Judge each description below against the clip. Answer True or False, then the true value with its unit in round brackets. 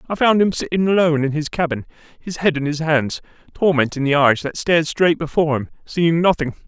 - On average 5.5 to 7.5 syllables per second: True (5.9 syllables/s)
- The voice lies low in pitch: False (155 Hz)